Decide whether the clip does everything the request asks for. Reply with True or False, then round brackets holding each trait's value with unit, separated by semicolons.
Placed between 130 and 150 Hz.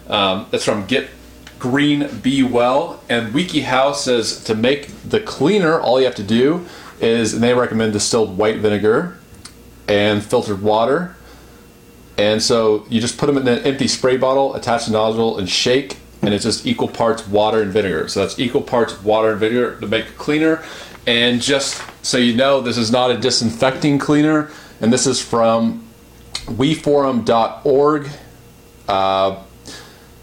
False (120 Hz)